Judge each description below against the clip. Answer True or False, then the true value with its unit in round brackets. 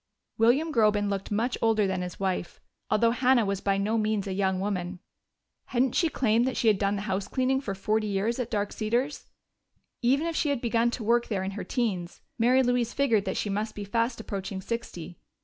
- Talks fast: True (210 wpm)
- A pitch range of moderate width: True (3.4 semitones)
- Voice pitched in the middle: False (215 Hz)